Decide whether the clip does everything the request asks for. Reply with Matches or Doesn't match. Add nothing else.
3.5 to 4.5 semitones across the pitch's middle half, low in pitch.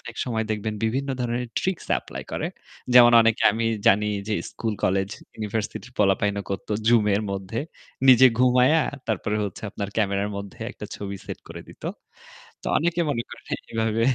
Doesn't match